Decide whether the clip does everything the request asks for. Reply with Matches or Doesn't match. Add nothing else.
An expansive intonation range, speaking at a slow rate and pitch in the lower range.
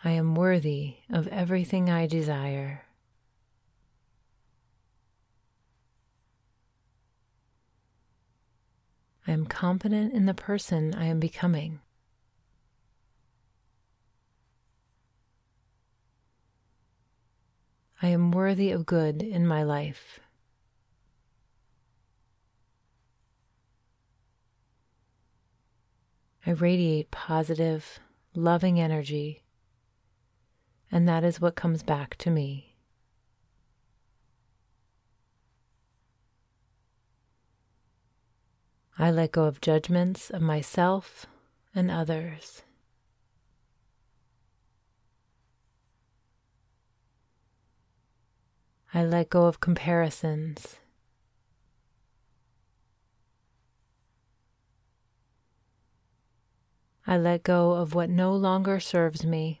Matches